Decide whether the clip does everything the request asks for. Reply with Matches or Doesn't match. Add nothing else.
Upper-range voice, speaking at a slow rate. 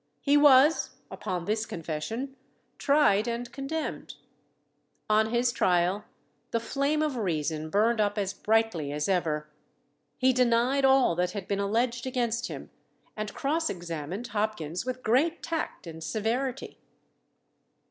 Matches